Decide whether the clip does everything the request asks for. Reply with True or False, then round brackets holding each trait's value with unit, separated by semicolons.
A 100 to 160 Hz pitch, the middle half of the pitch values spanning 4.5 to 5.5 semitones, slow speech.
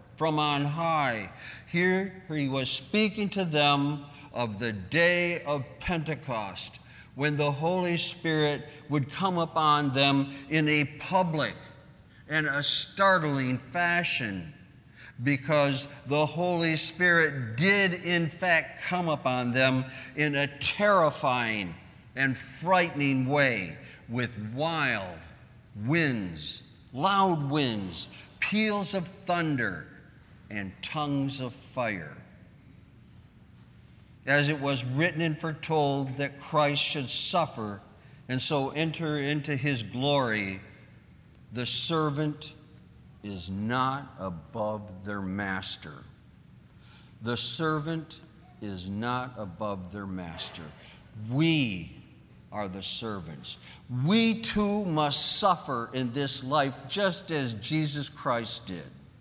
True (140 Hz; 5.1 semitones; 105 wpm)